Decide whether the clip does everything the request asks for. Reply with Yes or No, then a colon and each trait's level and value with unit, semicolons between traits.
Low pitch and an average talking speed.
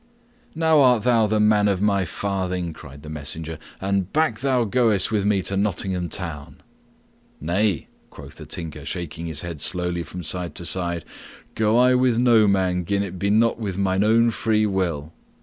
Yes: very low, 95 Hz; average, 180 wpm